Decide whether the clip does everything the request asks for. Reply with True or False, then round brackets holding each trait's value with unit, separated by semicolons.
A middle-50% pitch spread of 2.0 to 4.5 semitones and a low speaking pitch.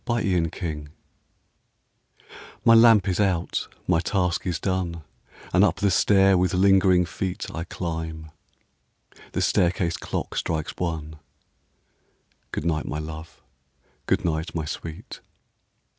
True (2.8 semitones; 85 Hz)